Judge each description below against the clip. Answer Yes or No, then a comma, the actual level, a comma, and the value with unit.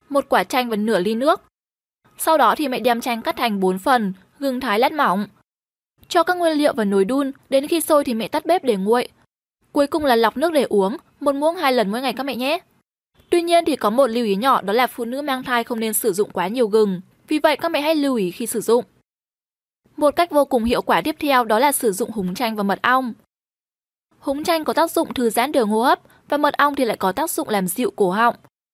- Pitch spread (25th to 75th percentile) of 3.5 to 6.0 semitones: Yes, average, 4.8 semitones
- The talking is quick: Yes, fast, 255 wpm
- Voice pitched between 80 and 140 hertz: No, very high, 255 Hz